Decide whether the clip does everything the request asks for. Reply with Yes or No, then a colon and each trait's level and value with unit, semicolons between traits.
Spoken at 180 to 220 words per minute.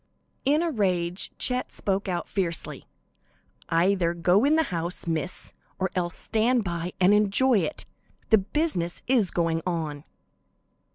No: slow, 135 wpm